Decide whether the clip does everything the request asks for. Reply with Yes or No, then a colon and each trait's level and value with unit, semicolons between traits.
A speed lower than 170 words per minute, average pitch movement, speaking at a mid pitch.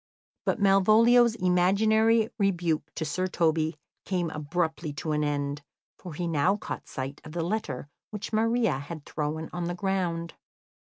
Yes: average, 150 wpm; average, 4.4 semitones; medium, 175 Hz